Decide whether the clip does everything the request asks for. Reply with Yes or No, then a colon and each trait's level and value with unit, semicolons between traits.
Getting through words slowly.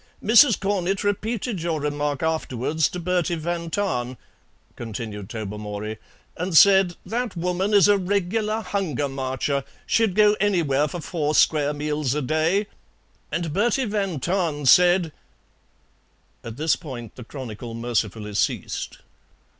Yes: slow, 130 wpm